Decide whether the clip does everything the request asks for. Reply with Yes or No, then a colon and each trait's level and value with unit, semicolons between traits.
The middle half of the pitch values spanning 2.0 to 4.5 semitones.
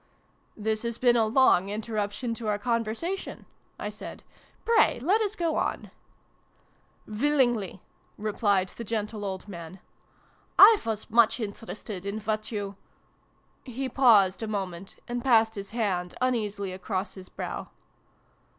Yes: average, 3.1 semitones